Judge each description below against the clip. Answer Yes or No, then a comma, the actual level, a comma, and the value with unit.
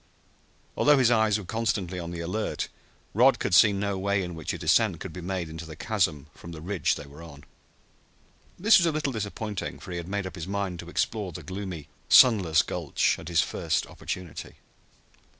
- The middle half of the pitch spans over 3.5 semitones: Yes, average, 3.9 semitones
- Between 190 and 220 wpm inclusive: Yes, average, 200 wpm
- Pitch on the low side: Yes, very low, 95 Hz